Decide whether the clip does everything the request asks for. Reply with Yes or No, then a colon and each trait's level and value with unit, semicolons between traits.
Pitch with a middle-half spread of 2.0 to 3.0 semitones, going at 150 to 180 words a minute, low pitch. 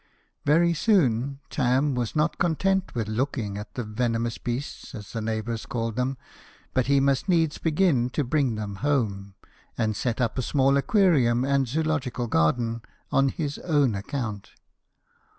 No: average, 4.2 semitones; average, 160 wpm; low, 130 Hz